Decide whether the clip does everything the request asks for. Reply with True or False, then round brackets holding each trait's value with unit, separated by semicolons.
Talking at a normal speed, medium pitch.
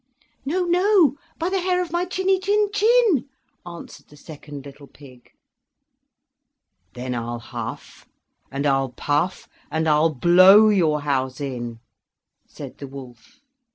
False (130 wpm; 160 Hz)